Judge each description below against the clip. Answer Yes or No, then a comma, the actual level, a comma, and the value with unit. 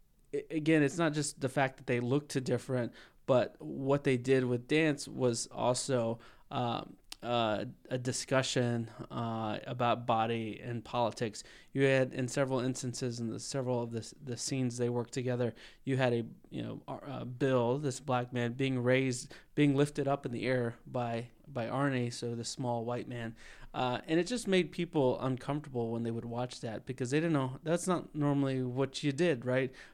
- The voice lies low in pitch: Yes, low, 130 Hz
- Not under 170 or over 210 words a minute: Yes, average, 185 wpm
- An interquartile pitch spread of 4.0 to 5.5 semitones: No, average, 2.7 semitones